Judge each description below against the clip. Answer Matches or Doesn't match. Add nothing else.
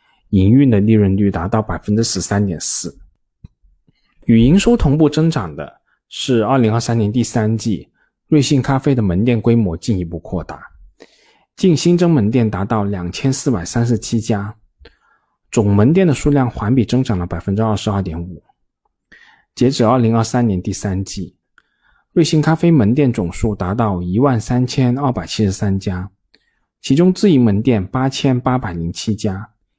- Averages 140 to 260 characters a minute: Matches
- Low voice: Matches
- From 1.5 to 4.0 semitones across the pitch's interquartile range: Doesn't match